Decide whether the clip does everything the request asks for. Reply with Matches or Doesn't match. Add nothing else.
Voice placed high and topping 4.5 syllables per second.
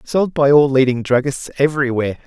Doesn't match